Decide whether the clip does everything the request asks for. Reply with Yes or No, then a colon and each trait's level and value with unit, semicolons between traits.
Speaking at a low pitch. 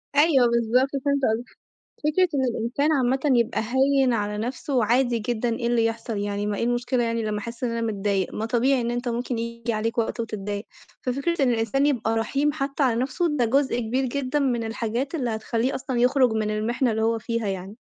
No: high, 235 Hz